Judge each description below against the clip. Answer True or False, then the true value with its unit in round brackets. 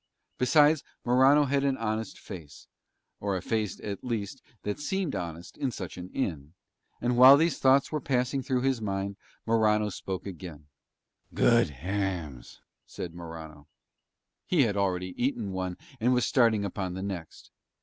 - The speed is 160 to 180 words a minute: False (150 wpm)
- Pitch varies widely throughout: True (5.8 semitones)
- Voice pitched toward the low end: True (105 Hz)